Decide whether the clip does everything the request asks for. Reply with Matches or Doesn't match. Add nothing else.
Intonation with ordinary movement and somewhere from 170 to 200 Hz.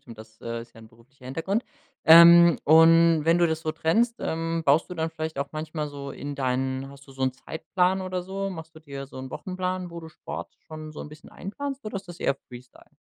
Doesn't match